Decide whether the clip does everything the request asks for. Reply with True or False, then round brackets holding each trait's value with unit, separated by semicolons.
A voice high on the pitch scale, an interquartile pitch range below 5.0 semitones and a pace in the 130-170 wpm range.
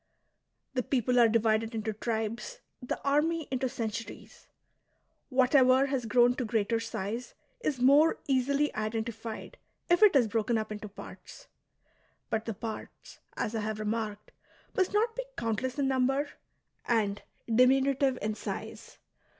True (240 Hz; 3.5 semitones; 135 wpm)